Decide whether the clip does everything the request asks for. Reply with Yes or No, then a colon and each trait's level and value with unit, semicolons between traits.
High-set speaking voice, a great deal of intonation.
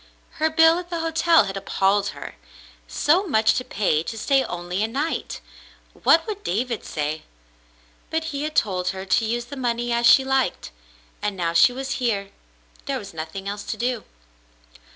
Yes: high, 235 Hz; wide, 7.0 semitones